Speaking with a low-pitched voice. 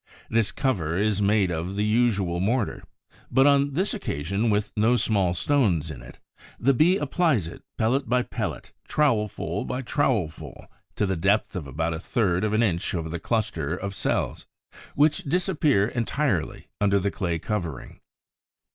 Yes: low, 105 Hz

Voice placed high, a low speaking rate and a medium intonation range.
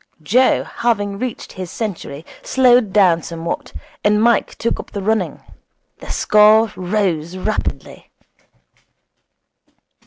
Yes: high, 210 Hz; slow, 105 wpm; average, 3.5 semitones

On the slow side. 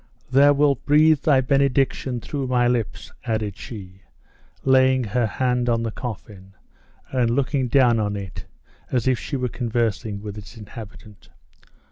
No: average, 145 wpm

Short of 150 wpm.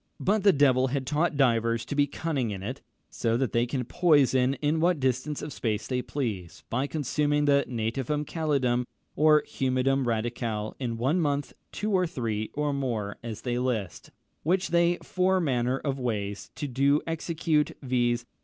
No: average, 165 wpm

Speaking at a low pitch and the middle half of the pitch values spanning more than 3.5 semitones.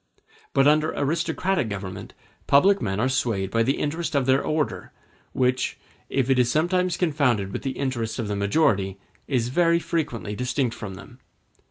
Yes: low, 130 Hz; wide, 5.4 semitones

